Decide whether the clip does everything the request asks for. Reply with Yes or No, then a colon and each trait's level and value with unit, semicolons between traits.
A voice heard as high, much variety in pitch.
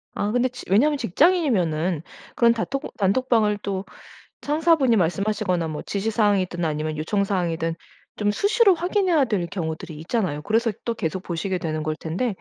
Yes: high, 205 Hz; wide, 6.5 semitones